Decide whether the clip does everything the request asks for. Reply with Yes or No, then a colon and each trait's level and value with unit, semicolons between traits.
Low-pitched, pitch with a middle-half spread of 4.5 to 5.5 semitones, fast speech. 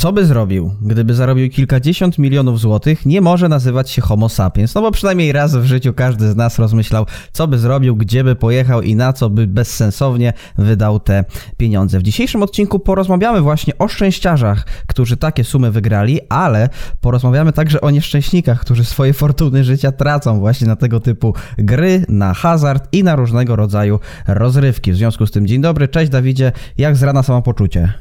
Yes: low, 125 Hz; average, 4.9 semitones; fast, 180 wpm